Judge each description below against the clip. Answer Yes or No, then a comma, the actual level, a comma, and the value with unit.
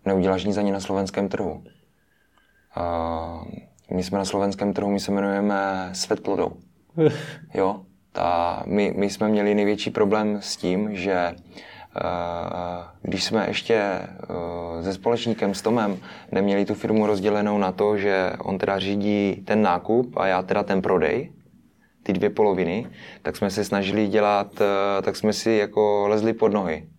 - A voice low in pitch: Yes, low, 100 Hz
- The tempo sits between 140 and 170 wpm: Yes, average, 155 wpm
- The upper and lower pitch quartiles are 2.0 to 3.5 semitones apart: No, narrow, 1.6 semitones